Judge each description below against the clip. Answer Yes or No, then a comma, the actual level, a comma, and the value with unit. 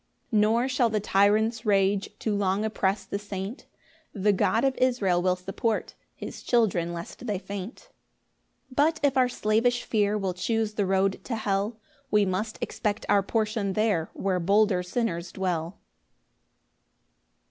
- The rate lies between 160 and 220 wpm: No, average, 150 wpm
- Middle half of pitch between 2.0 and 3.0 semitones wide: Yes, average, 2.7 semitones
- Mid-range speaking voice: No, high, 205 Hz